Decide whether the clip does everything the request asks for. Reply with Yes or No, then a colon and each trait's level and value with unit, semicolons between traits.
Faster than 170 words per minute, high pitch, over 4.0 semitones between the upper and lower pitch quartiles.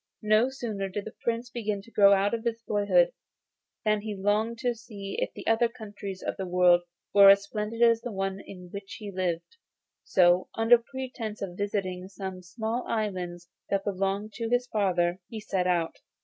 No: average, 180 wpm; high, 205 Hz; average, 3.0 semitones